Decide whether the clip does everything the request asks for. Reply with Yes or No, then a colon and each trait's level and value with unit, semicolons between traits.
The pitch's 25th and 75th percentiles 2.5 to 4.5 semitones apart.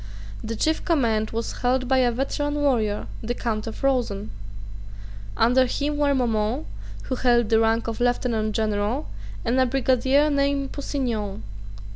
Yes: average, 3.5 semitones